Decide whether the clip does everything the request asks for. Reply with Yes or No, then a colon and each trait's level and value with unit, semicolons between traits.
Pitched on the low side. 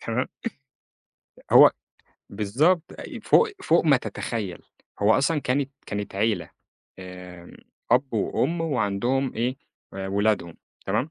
Yes: low, 115 Hz